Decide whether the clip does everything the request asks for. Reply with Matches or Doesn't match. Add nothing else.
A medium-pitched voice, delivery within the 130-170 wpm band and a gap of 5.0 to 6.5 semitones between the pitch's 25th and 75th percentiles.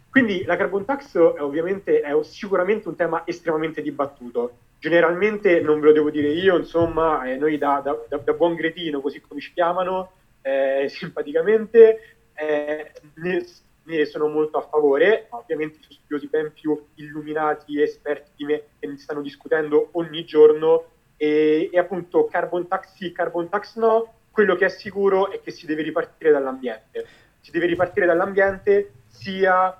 Doesn't match